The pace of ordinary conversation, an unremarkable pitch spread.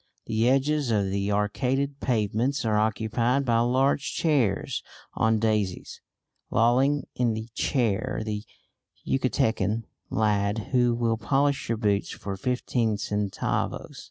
No: slow, 120 wpm; average, 3.5 semitones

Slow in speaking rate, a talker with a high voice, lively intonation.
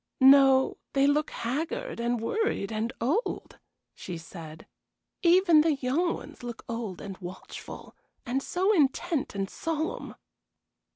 Yes: slow, 125 wpm; very high, 265 Hz; wide, 6.1 semitones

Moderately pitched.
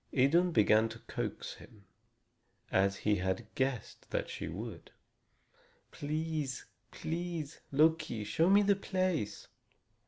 Yes: medium, 145 Hz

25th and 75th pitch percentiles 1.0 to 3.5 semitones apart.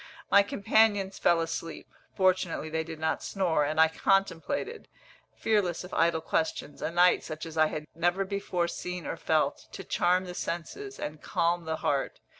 Yes: average, 3.1 semitones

